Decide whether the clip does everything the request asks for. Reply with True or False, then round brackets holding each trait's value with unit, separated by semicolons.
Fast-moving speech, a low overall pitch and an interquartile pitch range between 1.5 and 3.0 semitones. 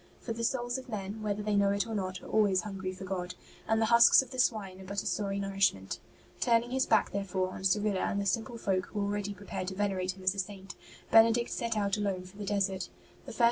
False (240 wpm; 200 Hz; 2.5 semitones)